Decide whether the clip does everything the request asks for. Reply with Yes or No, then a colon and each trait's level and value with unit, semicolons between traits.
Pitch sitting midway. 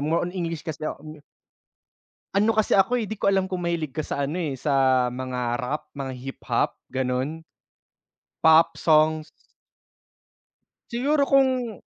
Yes: medium, 160 Hz